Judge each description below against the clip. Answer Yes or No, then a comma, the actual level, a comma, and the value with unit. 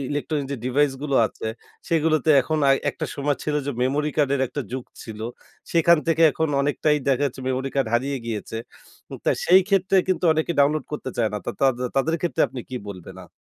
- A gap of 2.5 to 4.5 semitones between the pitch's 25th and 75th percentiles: Yes, average, 3.1 semitones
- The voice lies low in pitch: No, medium, 145 Hz